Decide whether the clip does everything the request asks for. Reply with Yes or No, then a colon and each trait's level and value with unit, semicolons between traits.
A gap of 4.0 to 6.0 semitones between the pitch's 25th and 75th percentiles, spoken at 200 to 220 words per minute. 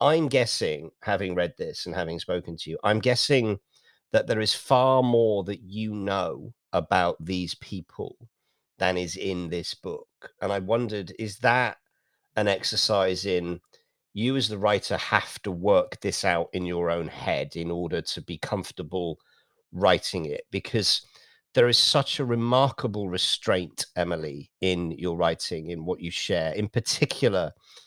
No: average, 5.0 semitones; average, 155 wpm